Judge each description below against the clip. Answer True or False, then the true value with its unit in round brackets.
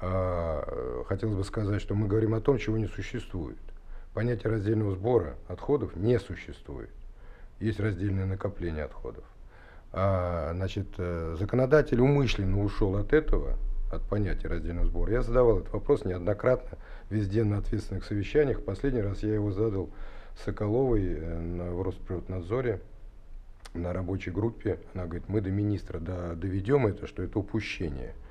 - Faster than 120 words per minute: True (130 wpm)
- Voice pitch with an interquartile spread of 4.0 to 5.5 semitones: False (3.4 semitones)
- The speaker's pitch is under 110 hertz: True (100 Hz)